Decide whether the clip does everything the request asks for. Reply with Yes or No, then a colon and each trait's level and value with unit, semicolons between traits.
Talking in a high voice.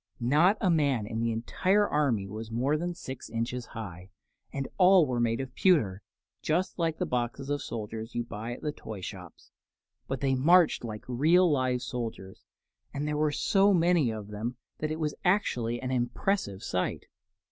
No: low, 130 Hz